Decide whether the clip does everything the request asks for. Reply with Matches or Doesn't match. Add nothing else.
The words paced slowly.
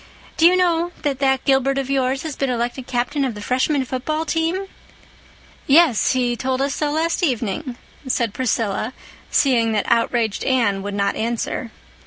Doesn't match